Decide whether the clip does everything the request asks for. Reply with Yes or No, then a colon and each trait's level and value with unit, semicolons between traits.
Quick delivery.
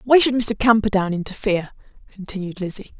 No: average, 140 wpm